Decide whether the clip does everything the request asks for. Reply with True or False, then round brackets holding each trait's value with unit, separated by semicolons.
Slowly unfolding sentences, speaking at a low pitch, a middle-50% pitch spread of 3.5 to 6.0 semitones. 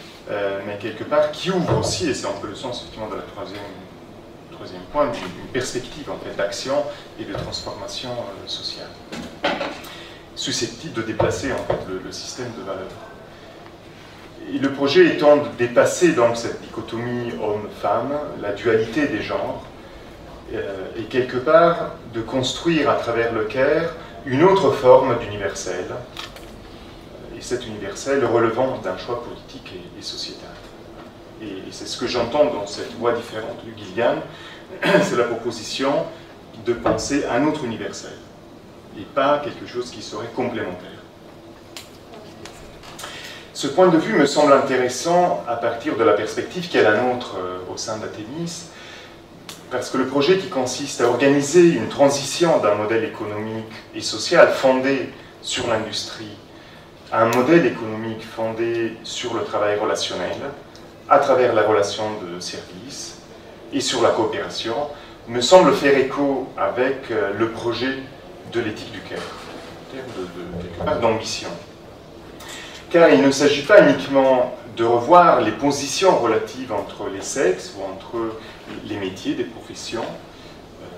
True (140 wpm; 120 Hz; 4.3 semitones)